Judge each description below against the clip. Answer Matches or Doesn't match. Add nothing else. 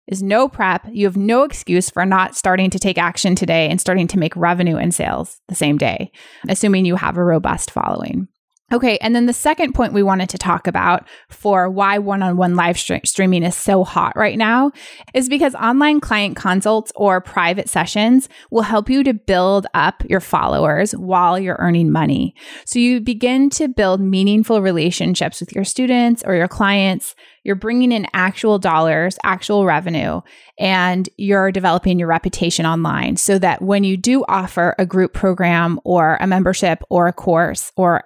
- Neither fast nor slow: Matches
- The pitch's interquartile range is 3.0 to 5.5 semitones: Matches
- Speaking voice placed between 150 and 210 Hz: Matches